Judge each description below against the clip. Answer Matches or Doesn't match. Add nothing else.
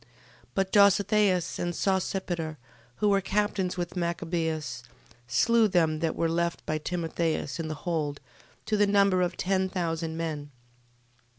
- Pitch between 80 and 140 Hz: Doesn't match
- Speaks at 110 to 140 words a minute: Matches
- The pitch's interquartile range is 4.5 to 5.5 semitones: Doesn't match